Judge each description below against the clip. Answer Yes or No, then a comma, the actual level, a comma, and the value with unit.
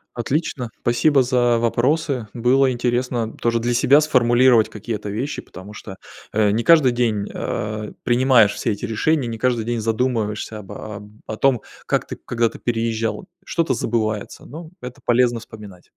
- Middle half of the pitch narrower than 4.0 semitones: Yes, average, 2.7 semitones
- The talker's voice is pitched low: Yes, low, 120 Hz